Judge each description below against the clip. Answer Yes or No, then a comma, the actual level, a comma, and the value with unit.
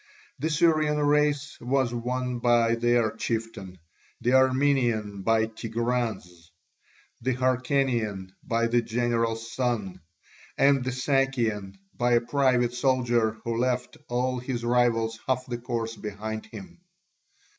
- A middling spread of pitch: No, narrow, 2.2 semitones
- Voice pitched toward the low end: Yes, low, 120 Hz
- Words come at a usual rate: No, slow, 120 wpm